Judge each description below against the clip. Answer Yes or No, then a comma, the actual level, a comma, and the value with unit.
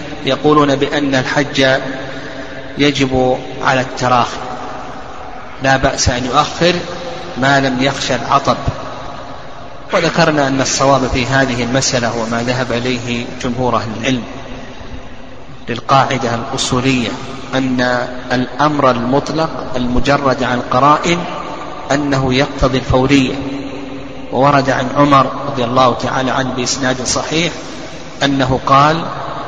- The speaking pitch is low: Yes, low, 130 Hz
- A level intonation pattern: Yes, narrow, 1.6 semitones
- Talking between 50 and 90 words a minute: No, average, 100 wpm